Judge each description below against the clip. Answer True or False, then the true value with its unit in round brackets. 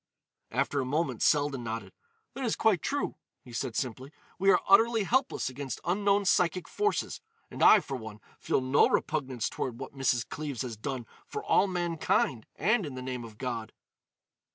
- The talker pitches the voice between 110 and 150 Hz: True (140 Hz)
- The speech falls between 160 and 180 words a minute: True (175 wpm)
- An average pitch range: False (6.9 semitones)